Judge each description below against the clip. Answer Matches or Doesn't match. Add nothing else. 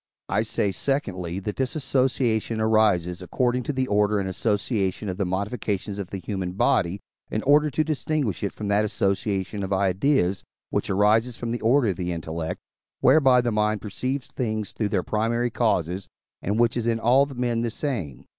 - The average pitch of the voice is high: Doesn't match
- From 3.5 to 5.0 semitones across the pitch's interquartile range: Matches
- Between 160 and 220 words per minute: Matches